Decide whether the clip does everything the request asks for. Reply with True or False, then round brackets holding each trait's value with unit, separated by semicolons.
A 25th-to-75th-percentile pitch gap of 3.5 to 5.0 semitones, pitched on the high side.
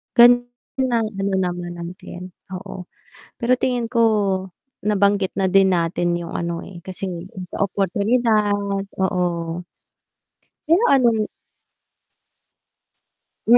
True (4.0 semitones; 195 Hz)